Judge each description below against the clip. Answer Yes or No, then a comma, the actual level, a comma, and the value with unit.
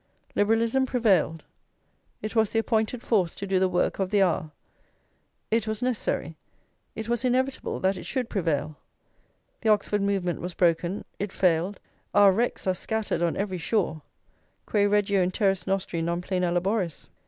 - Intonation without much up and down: No, average, 3.7 semitones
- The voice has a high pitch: Yes, high, 195 Hz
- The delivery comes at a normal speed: Yes, average, 160 wpm